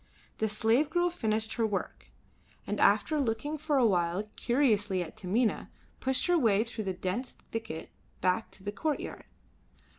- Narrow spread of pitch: No, average, 4.8 semitones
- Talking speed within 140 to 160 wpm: Yes, average, 155 wpm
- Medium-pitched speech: No, high, 220 Hz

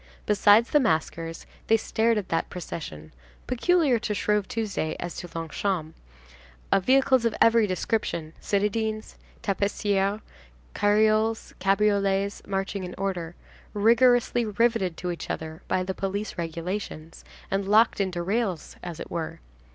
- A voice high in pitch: Yes, high, 195 Hz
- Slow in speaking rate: Yes, slow, 125 wpm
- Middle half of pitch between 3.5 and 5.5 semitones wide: Yes, average, 4.3 semitones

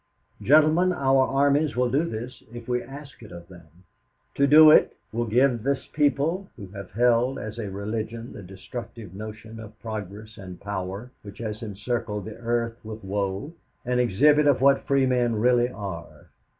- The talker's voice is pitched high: No, low, 115 Hz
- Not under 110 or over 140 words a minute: No, average, 170 wpm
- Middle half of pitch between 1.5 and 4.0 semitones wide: No, average, 4.4 semitones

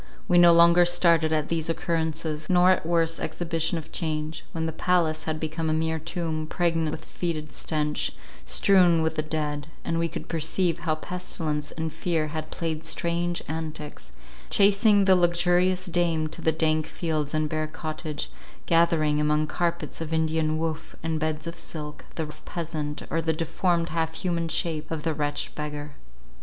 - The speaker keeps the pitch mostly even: Yes, narrow, 1.6 semitones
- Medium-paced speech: Yes, average, 170 wpm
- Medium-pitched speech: Yes, medium, 160 Hz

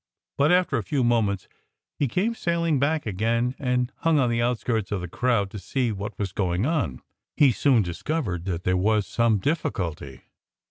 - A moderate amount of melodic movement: No, wide, 6.3 semitones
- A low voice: Yes, low, 115 Hz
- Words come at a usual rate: Yes, average, 180 wpm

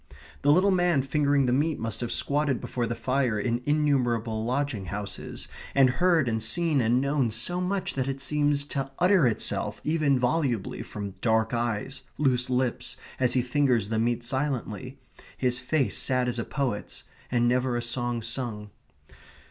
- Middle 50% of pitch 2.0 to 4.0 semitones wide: Yes, average, 3.4 semitones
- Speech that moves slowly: No, average, 165 wpm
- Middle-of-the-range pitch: No, low, 125 Hz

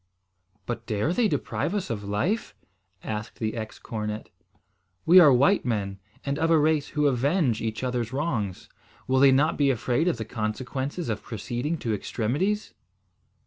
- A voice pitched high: No, low, 130 Hz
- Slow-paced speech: No, average, 160 wpm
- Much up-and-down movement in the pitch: Yes, wide, 5.7 semitones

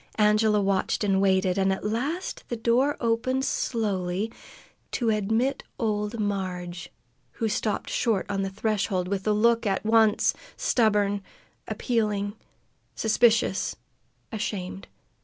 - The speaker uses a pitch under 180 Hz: No, high, 210 Hz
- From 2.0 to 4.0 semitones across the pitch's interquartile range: Yes, average, 2.7 semitones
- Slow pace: Yes, slow, 120 wpm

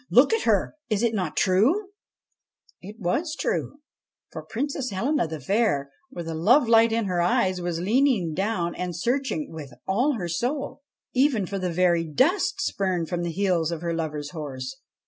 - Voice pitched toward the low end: No, high, 190 Hz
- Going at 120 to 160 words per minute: No, average, 175 wpm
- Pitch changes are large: Yes, wide, 6.6 semitones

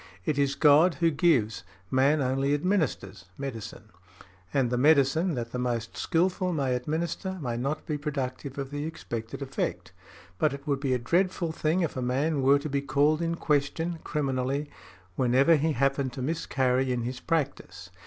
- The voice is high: No, medium, 140 Hz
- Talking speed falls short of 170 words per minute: No, average, 175 wpm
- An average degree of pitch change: Yes, average, 3.6 semitones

